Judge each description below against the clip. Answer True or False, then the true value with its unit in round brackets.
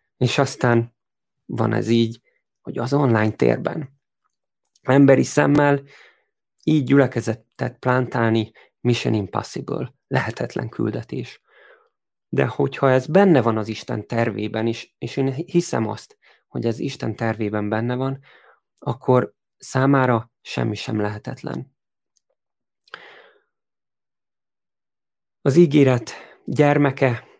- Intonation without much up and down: False (3.8 semitones)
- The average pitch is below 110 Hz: False (125 Hz)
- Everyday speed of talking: False (100 wpm)